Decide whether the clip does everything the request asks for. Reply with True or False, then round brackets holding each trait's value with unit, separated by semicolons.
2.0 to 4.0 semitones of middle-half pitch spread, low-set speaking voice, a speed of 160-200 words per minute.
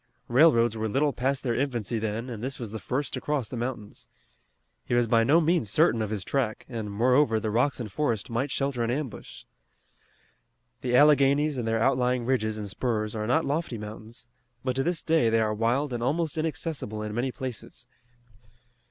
True (3.7 semitones; 120 Hz; 190 wpm)